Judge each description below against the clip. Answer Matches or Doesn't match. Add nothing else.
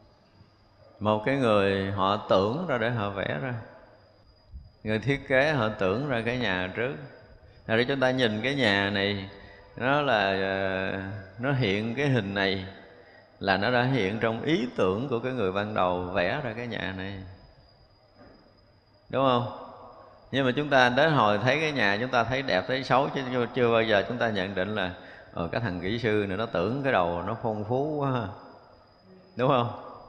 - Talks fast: Doesn't match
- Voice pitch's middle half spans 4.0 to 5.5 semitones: Matches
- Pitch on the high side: Doesn't match